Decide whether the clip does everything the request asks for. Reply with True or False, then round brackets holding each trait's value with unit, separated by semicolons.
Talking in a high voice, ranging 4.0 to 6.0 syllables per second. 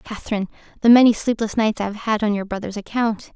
False (215 Hz; 6.4 syllables/s)